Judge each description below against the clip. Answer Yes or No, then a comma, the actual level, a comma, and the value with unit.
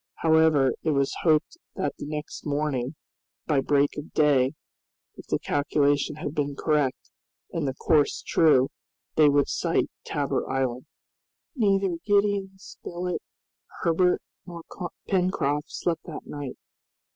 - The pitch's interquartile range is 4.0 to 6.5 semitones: No, average, 3.1 semitones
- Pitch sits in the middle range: Yes, medium, 150 Hz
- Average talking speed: No, slow, 125 wpm